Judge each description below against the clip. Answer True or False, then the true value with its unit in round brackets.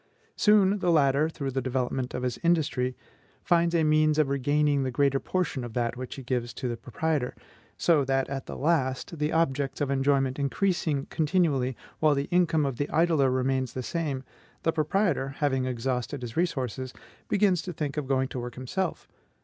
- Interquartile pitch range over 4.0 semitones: False (3.7 semitones)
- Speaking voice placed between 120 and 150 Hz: True (140 Hz)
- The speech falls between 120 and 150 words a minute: False (180 wpm)